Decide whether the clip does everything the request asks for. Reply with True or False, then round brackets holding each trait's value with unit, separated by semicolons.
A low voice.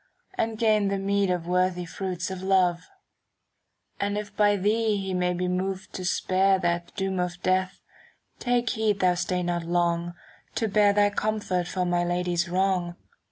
False (185 Hz)